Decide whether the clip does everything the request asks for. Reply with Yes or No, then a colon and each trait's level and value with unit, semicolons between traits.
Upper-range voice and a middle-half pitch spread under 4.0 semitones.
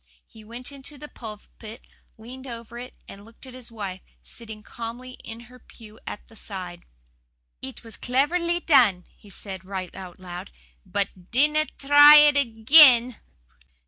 No: high, 230 Hz; average, 4.4 semitones